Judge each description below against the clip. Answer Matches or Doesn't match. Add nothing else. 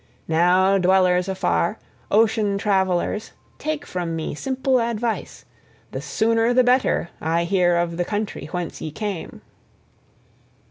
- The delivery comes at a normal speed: Doesn't match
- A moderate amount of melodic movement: Matches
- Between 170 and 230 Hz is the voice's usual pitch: Matches